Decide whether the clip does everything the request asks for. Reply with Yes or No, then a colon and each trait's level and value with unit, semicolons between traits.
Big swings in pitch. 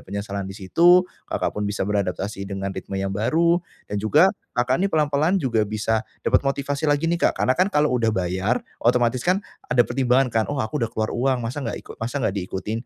Yes: wide, 5.8 semitones